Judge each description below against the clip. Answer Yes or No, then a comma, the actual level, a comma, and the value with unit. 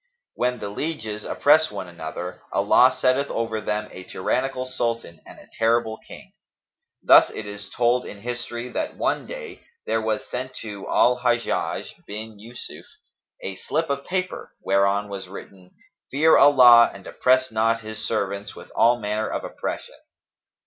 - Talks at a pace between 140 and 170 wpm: Yes, average, 155 wpm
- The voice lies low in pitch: Yes, low, 115 Hz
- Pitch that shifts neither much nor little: Yes, average, 3.7 semitones